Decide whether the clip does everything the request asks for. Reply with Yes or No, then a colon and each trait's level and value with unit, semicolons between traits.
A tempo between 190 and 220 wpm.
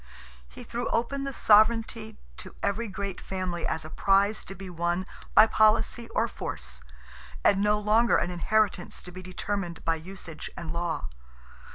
No: average, 160 wpm